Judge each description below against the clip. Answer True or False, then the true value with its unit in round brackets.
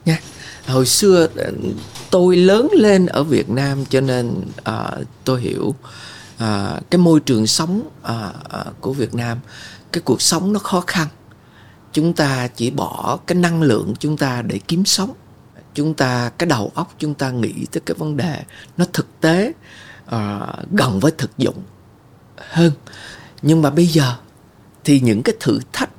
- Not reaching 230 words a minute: True (165 wpm)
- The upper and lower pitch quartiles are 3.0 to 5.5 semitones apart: False (5.9 semitones)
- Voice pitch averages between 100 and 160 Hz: True (140 Hz)